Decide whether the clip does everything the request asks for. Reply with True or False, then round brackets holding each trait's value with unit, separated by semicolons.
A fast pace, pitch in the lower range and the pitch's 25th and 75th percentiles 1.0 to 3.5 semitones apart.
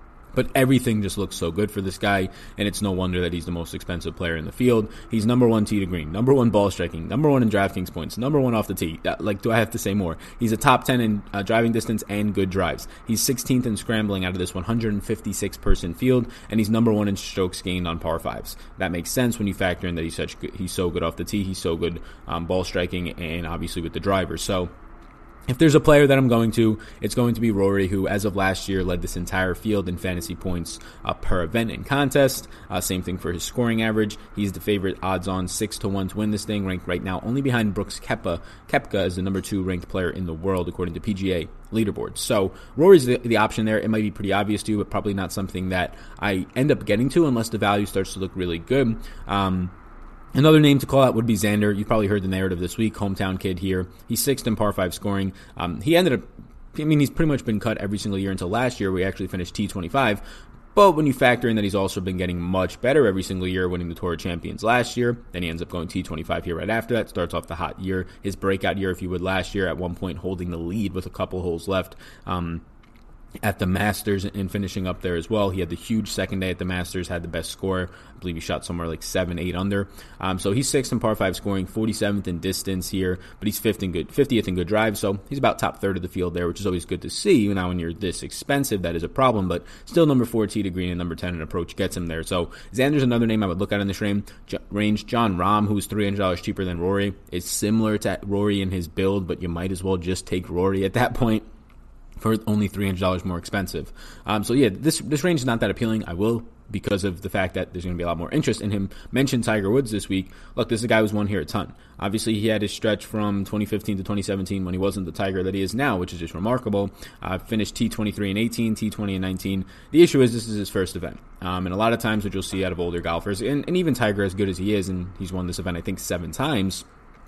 True (265 wpm; 100 Hz; 3.2 semitones)